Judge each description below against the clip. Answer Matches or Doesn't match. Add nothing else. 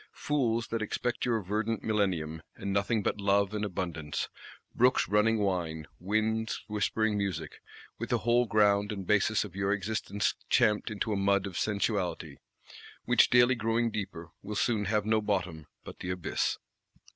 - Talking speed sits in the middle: Matches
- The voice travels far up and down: Doesn't match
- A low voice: Matches